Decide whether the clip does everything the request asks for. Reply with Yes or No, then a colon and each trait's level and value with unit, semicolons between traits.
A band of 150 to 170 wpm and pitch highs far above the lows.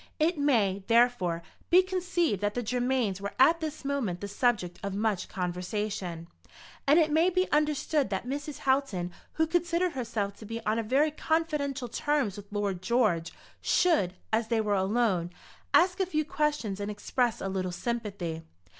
Yes: average, 165 wpm; wide, 7.2 semitones